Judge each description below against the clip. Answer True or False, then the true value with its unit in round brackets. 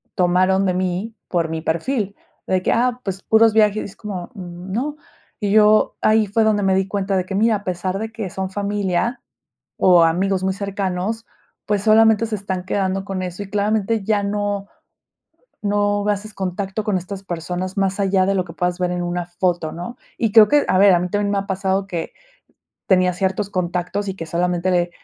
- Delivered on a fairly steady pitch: True (2.3 semitones)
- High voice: True (195 Hz)